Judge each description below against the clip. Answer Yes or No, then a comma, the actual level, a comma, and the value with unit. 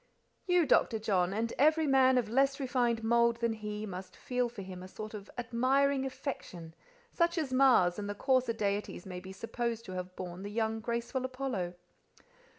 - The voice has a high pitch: Yes, high, 230 Hz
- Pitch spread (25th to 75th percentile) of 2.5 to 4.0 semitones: No, average, 4.4 semitones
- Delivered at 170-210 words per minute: Yes, average, 185 wpm